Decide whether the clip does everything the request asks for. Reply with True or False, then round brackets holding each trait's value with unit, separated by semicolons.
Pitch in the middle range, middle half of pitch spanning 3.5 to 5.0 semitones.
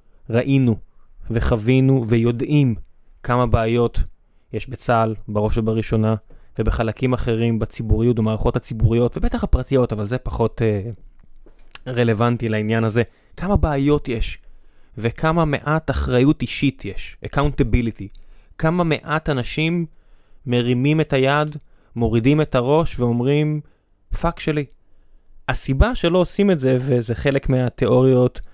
False (120 Hz; 4.0 semitones)